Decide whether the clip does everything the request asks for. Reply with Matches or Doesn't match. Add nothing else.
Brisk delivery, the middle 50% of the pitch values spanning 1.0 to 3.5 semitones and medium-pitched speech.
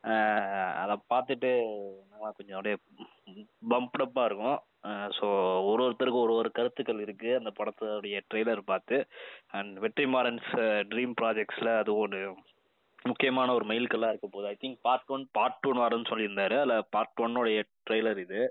Doesn't match